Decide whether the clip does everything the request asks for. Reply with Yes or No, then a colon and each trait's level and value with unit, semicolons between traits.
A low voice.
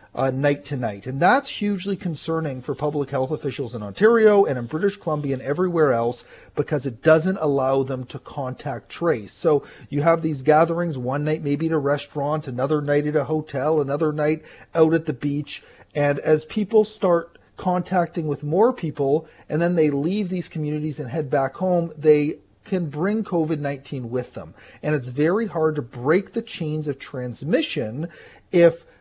No: medium, 155 Hz